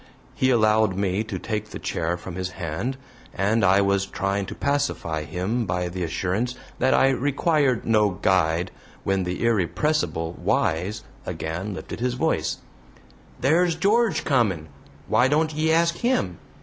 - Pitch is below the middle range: Yes, low, 105 Hz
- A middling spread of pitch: No, wide, 6.6 semitones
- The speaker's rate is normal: Yes, average, 150 wpm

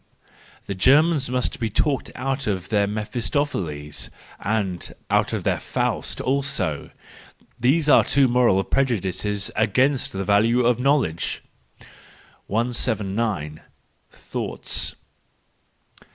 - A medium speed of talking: No, slow, 95 wpm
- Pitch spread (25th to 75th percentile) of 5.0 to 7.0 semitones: Yes, average, 5.3 semitones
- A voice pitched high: No, low, 115 Hz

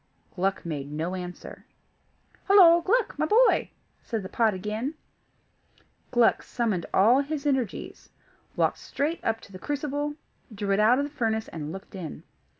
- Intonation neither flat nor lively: No, wide, 7.3 semitones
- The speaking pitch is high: Yes, high, 225 Hz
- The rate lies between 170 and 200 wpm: No, average, 150 wpm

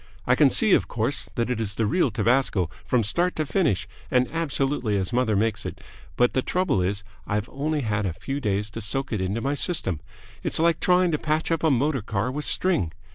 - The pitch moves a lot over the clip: Yes, wide, 6.6 semitones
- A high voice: No, low, 125 Hz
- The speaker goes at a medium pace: No, fast, 220 wpm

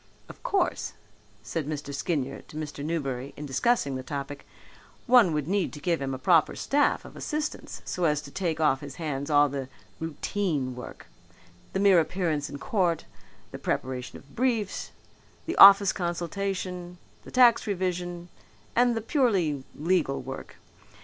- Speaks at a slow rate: No, average, 155 wpm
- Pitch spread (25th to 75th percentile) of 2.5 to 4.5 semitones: No, wide, 5.6 semitones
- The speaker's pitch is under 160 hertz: No, medium, 165 Hz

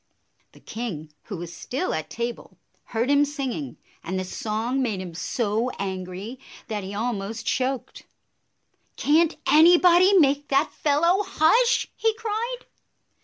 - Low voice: No, very high, 255 Hz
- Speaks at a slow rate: Yes, slow, 130 wpm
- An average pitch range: No, wide, 7.7 semitones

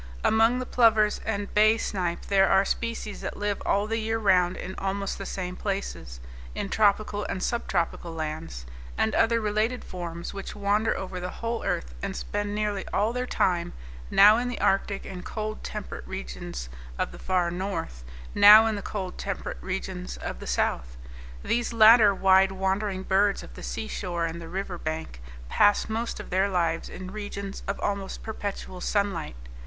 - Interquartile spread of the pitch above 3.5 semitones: No, average, 3.0 semitones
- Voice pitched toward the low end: No, high, 195 Hz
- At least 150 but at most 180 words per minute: Yes, average, 170 wpm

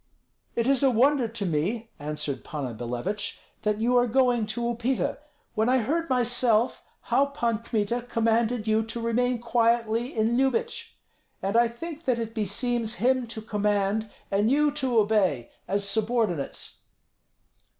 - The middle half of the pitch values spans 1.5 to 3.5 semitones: Yes, average, 2.8 semitones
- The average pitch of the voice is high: Yes, high, 230 Hz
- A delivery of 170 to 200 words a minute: No, average, 150 wpm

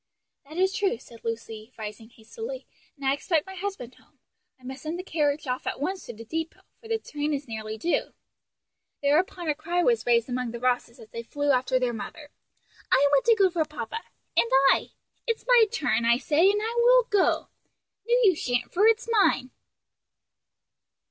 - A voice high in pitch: Yes, very high, 290 Hz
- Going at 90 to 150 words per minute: No, average, 190 wpm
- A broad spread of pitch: Yes, wide, 7.9 semitones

